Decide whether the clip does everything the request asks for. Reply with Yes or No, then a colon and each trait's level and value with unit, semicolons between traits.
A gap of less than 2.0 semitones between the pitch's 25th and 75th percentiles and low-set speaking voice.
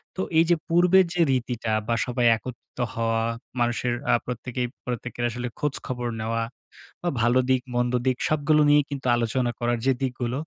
No: average, 2.8 semitones; low, 125 Hz